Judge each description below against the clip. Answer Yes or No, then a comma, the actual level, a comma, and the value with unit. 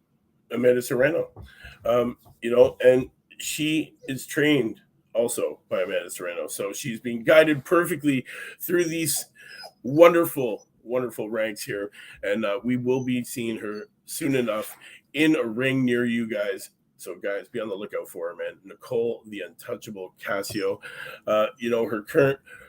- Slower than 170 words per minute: Yes, average, 150 wpm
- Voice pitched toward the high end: No, low, 135 Hz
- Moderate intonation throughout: No, wide, 6.7 semitones